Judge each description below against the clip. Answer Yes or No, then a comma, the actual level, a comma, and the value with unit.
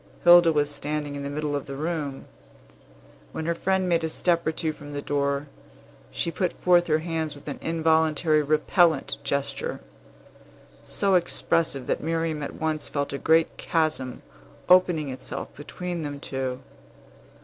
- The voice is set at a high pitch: No, medium, 155 Hz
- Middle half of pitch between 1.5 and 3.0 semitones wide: Yes, narrow, 2.6 semitones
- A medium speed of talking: Yes, average, 155 wpm